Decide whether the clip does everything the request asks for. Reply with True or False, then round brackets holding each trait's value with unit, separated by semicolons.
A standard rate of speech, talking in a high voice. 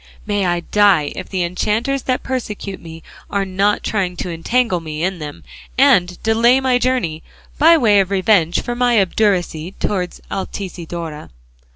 True (155 wpm; 195 Hz)